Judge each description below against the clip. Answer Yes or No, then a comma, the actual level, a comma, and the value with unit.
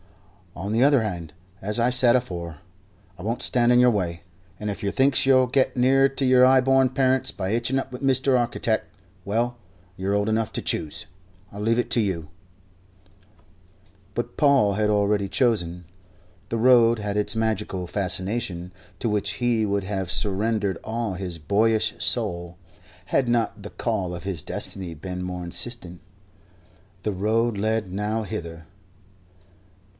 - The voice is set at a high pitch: No, low, 105 Hz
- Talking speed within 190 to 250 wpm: No, average, 155 wpm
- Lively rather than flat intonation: No, average, 4.4 semitones